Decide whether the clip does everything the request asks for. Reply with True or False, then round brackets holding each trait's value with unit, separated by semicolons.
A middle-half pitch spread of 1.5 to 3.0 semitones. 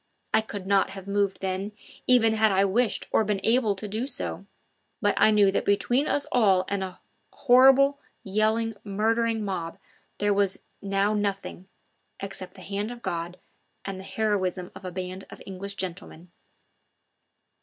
True (2.5 semitones)